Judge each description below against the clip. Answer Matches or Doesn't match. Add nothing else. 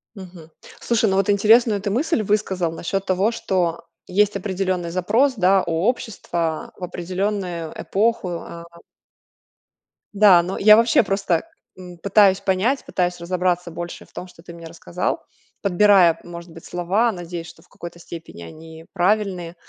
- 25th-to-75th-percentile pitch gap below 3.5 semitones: Matches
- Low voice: Doesn't match